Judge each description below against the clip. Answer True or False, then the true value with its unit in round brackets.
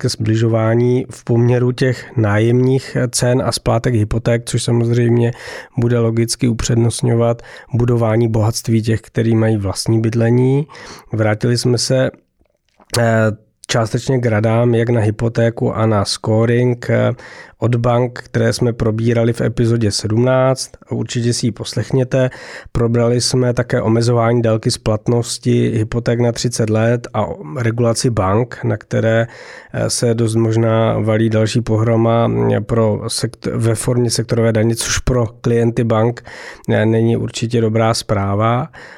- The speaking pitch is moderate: False (115 Hz)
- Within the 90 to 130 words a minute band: True (125 wpm)